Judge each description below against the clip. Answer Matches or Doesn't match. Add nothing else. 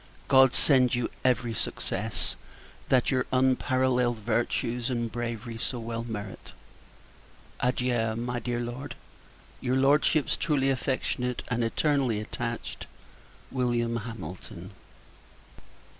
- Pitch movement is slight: Matches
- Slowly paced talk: Matches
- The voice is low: Matches